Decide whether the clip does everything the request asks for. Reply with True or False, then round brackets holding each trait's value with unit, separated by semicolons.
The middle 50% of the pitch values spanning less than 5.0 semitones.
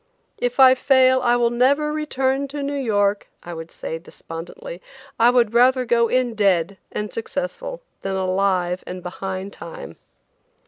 False (5.5 semitones)